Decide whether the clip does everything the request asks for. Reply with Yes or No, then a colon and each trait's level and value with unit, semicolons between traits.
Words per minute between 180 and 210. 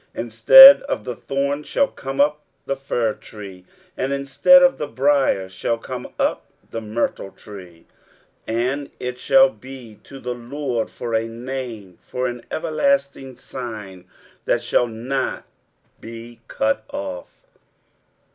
No: slow, 135 wpm